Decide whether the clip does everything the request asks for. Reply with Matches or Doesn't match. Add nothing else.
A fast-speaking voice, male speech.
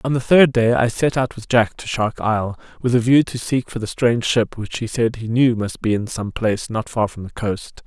Matches